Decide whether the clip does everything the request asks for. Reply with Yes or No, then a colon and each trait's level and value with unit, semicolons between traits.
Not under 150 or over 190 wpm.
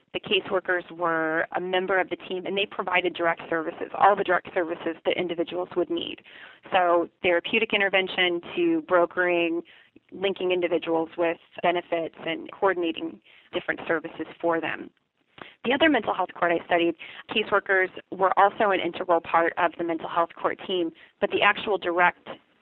Yes: average, 155 wpm